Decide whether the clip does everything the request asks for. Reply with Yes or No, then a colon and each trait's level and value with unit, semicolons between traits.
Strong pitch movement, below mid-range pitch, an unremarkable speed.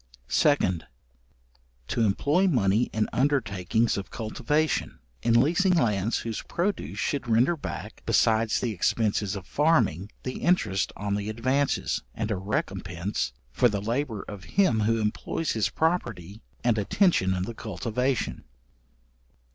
No: wide, 5.8 semitones; low, 115 Hz; slow, 130 wpm